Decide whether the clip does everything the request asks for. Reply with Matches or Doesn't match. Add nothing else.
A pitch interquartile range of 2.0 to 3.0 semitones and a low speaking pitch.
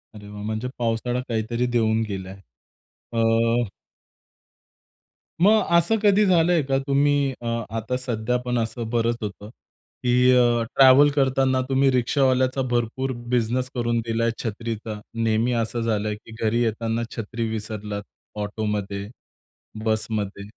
Matches